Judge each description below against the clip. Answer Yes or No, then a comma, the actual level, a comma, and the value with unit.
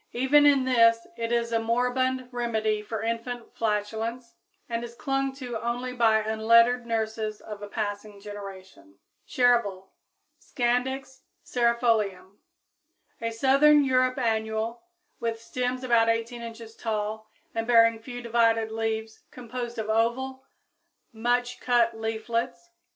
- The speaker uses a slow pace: Yes, slow, 125 wpm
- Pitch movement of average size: No, narrow, 2.0 semitones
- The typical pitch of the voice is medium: No, high, 230 Hz